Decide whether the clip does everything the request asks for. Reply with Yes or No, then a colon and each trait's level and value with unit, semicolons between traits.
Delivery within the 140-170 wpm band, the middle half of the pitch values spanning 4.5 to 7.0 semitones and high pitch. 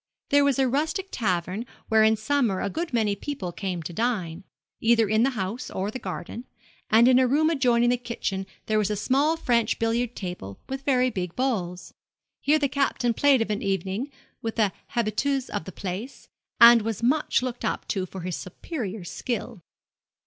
No: average, 185 wpm; average, 5.1 semitones; high, 230 Hz